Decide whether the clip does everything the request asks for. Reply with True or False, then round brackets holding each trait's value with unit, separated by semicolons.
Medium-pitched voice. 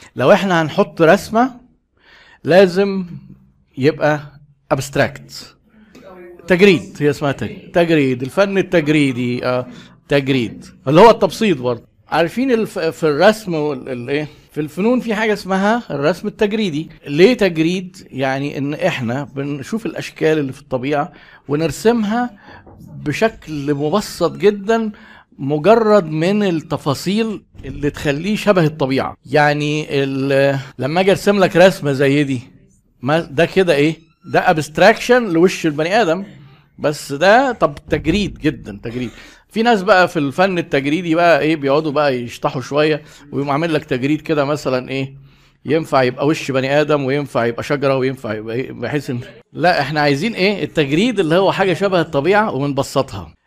True (155 Hz)